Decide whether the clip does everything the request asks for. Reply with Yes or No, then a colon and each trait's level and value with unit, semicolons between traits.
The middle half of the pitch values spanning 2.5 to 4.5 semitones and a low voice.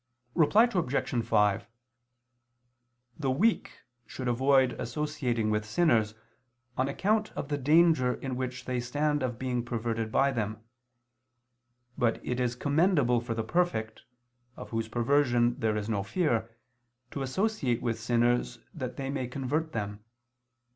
Yes: average, 3.8 semitones; low, 125 Hz